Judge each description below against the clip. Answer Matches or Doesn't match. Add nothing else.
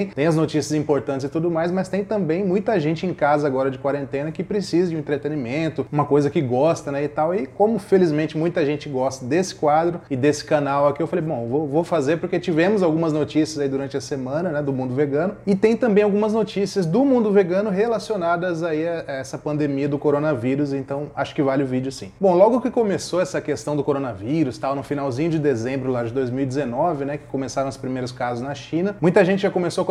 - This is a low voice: Doesn't match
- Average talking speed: Doesn't match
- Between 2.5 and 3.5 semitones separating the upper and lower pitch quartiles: Doesn't match